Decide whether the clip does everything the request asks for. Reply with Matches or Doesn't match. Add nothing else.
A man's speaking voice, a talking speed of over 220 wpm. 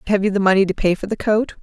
Doesn't match